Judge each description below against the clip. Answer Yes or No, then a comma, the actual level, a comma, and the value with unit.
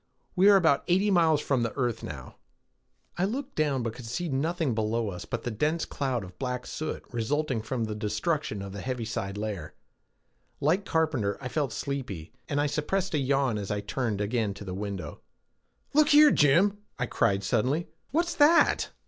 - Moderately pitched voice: No, low, 130 Hz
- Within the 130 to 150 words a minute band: No, average, 180 wpm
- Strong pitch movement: Yes, wide, 7.0 semitones